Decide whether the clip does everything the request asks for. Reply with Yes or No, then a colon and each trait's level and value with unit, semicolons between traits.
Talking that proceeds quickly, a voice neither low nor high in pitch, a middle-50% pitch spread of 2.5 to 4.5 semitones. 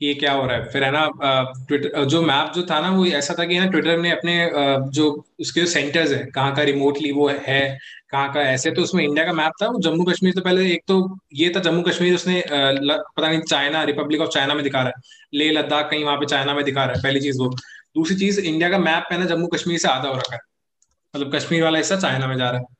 Yes: fast, 265 wpm; medium, 150 Hz; average, 3.5 semitones